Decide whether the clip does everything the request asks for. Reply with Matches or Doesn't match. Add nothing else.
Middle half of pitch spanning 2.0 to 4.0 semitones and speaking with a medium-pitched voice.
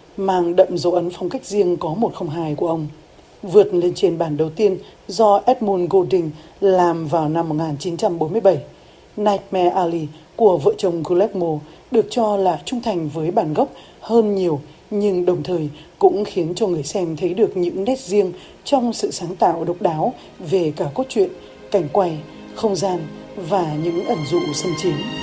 Matches